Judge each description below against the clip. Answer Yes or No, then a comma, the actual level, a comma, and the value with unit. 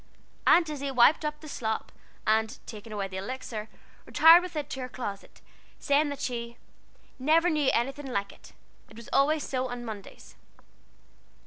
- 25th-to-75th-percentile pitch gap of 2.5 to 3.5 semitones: No, average, 5.2 semitones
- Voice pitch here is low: No, very high, 255 Hz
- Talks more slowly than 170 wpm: Yes, average, 160 wpm